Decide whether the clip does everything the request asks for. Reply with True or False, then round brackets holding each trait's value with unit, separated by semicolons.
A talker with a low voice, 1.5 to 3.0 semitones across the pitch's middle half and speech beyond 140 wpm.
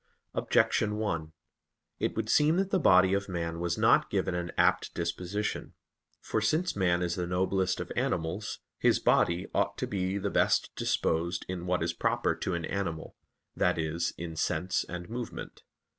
True (90 Hz; 2.7 semitones; 170 wpm)